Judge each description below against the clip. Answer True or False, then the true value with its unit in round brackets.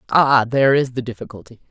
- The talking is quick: False (175 wpm)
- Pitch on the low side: True (125 Hz)